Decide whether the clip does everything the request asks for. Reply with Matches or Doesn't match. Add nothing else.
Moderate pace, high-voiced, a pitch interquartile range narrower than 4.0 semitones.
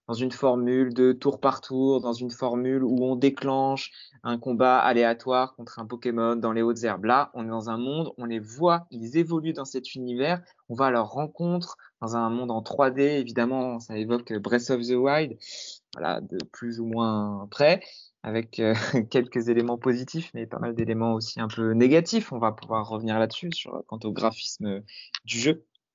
Doesn't match